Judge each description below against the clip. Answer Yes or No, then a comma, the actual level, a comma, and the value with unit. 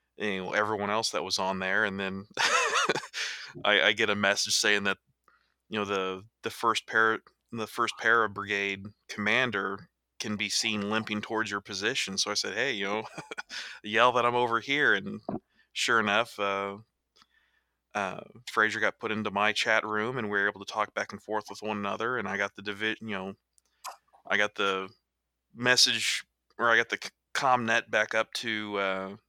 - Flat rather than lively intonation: Yes, narrow, 1.8 semitones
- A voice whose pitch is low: Yes, low, 105 Hz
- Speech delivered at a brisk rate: No, average, 190 wpm